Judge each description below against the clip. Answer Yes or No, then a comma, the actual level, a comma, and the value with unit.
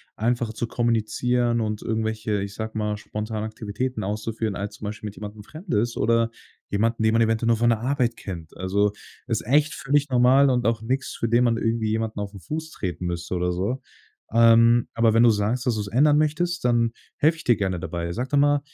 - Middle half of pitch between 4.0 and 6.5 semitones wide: No, average, 2.7 semitones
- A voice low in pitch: Yes, low, 115 Hz